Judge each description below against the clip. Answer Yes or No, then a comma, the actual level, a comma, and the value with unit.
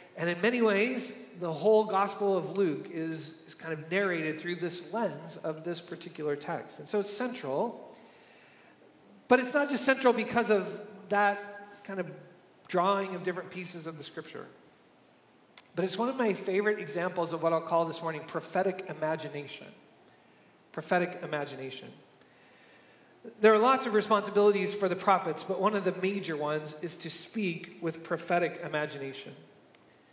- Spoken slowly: No, average, 155 wpm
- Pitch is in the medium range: Yes, medium, 180 Hz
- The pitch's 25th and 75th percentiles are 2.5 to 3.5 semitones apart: No, average, 3.9 semitones